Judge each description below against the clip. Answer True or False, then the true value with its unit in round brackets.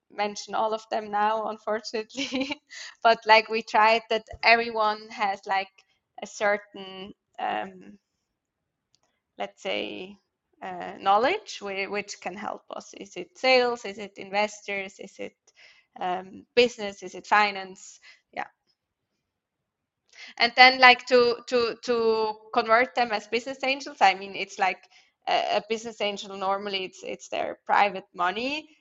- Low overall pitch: False (215 Hz)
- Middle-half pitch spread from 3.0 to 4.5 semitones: True (3.3 semitones)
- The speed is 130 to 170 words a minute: True (135 wpm)